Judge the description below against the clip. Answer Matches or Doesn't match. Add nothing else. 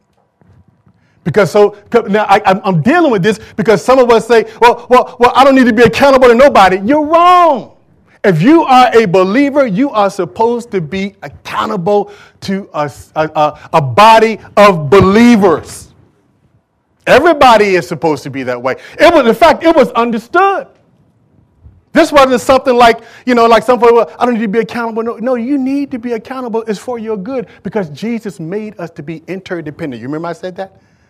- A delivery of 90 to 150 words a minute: Doesn't match